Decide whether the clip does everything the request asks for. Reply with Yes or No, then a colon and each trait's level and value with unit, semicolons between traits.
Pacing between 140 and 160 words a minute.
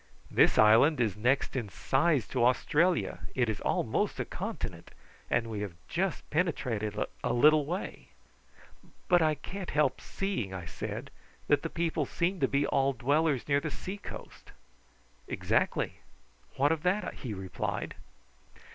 Yes: average, 145 wpm